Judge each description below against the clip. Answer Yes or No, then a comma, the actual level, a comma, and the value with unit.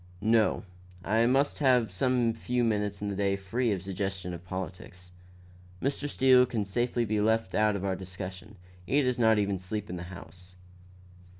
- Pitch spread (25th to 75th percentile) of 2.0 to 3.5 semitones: No, average, 4.2 semitones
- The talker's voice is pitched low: Yes, low, 105 Hz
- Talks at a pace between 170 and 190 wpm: Yes, average, 180 wpm